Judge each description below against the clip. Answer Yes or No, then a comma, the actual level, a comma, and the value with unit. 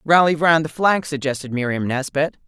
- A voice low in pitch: No, medium, 150 Hz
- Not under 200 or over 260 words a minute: No, average, 170 wpm